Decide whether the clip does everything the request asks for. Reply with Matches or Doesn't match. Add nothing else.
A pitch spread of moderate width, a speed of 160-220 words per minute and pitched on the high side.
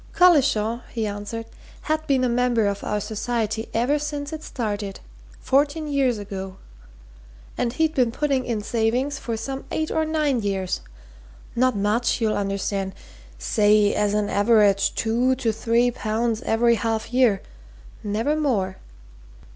Doesn't match